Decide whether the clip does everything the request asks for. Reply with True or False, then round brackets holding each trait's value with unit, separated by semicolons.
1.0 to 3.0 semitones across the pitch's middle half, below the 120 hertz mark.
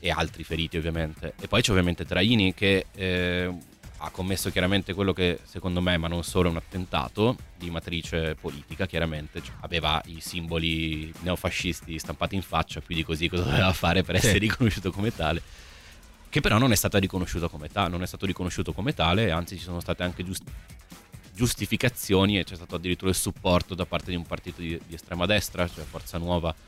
True (2.4 semitones; 90 Hz)